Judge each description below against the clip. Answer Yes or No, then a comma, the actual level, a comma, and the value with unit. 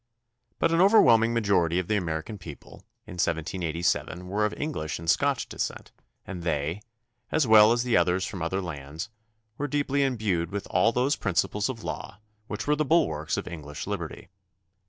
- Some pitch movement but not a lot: No, wide, 5.9 semitones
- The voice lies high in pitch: No, low, 100 Hz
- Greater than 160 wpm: Yes, average, 175 wpm